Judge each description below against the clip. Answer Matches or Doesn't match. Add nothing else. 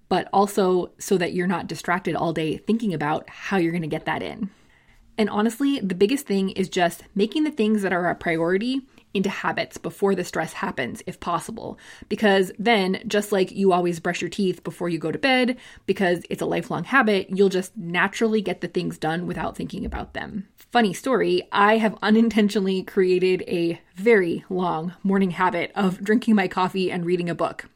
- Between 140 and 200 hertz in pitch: Matches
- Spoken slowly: Doesn't match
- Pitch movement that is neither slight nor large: Matches